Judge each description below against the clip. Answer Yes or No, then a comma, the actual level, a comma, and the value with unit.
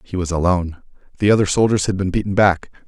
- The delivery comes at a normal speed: No, fast, 210 wpm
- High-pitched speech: No, very low, 95 Hz